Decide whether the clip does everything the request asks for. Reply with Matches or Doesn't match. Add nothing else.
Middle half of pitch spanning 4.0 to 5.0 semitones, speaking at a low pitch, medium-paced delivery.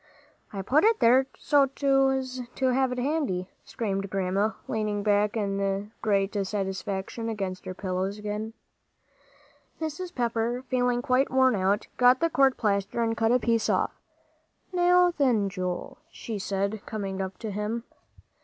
Doesn't match